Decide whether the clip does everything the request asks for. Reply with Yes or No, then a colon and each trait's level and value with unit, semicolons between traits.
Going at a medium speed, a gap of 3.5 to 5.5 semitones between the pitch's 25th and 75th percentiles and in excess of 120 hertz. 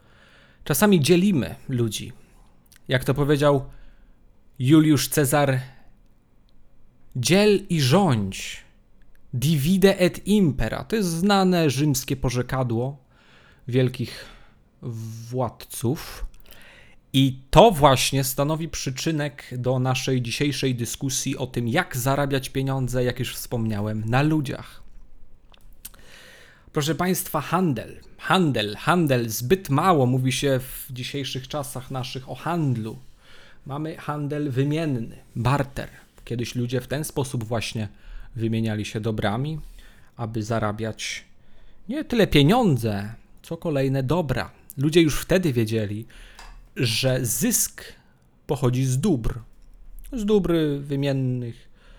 No: slow, 100 wpm; average, 4.6 semitones; low, 135 Hz